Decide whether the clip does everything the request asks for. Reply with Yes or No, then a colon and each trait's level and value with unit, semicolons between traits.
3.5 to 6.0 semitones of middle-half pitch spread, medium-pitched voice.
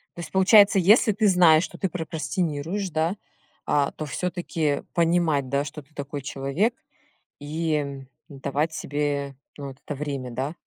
Yes: average, 3.8 semitones; medium, 155 Hz